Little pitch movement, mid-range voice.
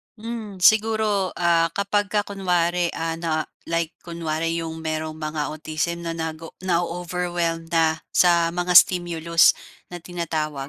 Yes: narrow, 1.6 semitones; medium, 170 Hz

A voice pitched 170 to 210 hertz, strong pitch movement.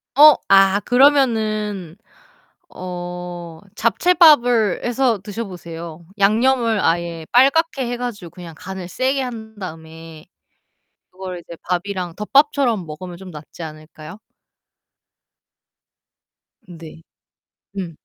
Yes: high, 190 Hz; wide, 5.9 semitones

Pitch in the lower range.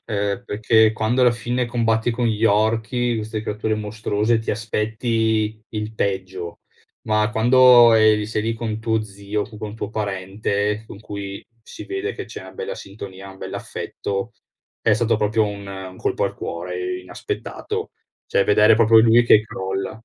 Yes: low, 110 Hz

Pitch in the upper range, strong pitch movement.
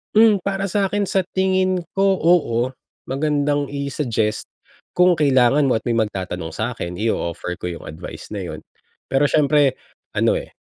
No: medium, 140 Hz; wide, 8.2 semitones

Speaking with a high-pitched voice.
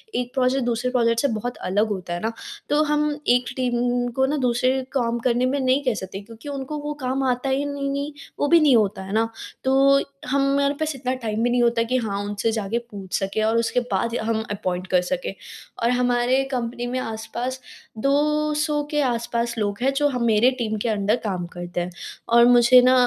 Yes: high, 245 Hz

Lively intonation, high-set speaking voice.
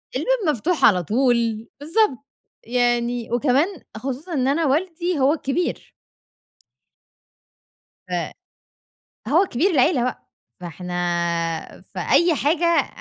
Yes: wide, 5.8 semitones; very high, 275 Hz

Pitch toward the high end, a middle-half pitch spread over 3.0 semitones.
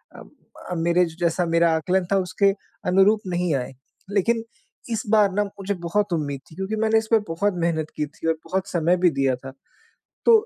No: medium, 180 Hz; average, 3.6 semitones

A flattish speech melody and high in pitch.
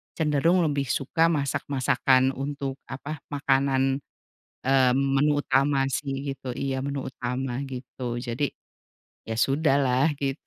No: narrow, 1.3 semitones; low, 135 Hz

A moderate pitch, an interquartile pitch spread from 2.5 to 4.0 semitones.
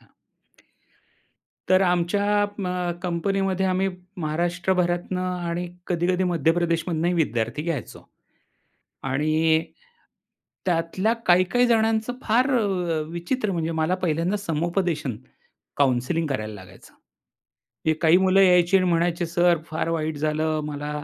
Yes: medium, 175 Hz; average, 2.8 semitones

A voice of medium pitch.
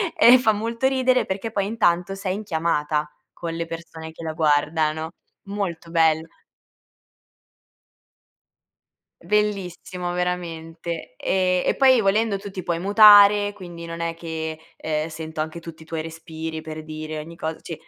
Yes: medium, 170 Hz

